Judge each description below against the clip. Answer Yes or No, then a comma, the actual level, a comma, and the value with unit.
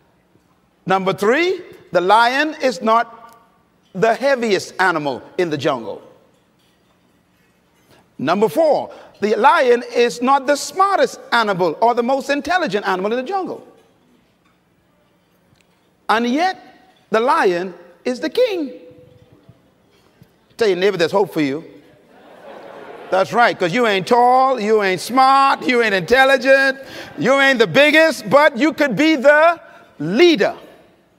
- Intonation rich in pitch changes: Yes, wide, 7.4 semitones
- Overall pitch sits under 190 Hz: No, high, 245 Hz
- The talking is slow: Yes, slow, 125 wpm